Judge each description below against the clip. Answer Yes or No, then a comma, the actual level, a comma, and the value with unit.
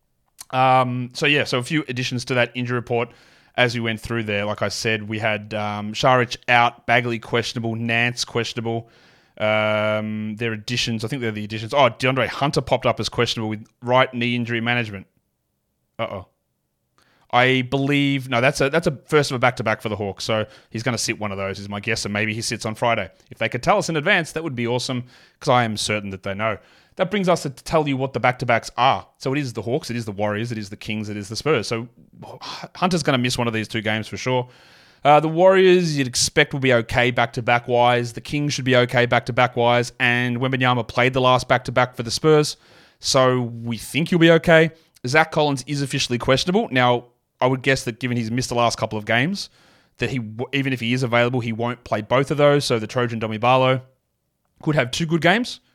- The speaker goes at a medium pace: No, fast, 235 wpm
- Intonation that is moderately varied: Yes, average, 3.0 semitones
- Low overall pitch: Yes, low, 120 Hz